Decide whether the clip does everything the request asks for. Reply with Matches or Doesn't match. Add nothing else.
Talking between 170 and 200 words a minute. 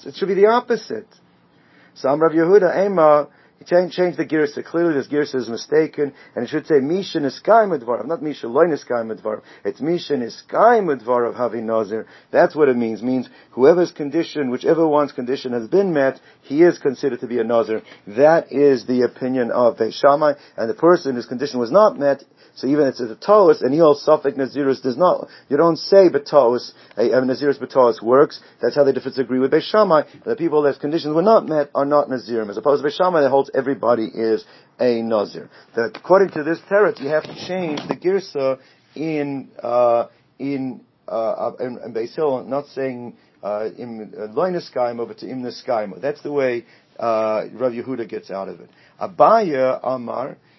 Matches